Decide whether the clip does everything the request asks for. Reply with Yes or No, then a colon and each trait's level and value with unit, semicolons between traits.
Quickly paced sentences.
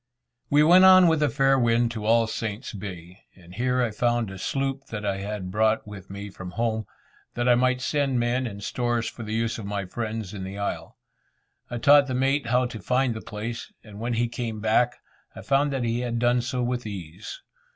Yes: fast, 215 wpm